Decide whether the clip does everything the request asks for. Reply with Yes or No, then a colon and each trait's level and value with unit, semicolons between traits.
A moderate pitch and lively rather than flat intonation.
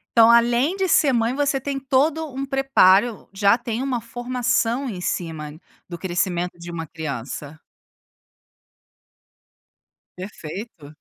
No: high, 230 Hz; wide, 7.1 semitones